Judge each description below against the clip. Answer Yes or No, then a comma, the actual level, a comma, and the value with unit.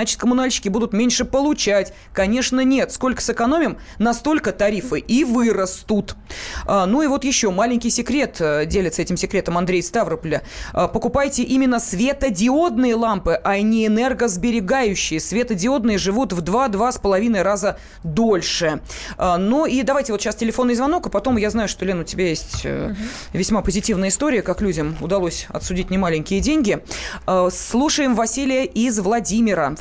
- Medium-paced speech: Yes, average, 135 wpm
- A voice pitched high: Yes, high, 220 Hz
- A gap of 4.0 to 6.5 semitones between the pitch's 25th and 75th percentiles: Yes, average, 4.7 semitones